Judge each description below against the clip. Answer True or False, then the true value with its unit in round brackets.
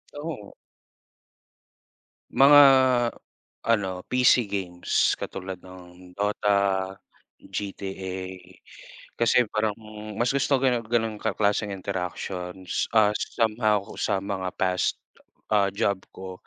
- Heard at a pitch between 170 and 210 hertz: False (100 Hz)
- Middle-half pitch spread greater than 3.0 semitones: False (2.7 semitones)